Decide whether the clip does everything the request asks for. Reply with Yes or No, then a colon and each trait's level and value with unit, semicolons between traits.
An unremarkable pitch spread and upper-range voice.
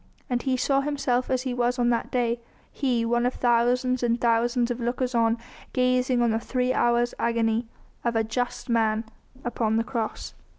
No: narrow, 1.4 semitones; high, 240 Hz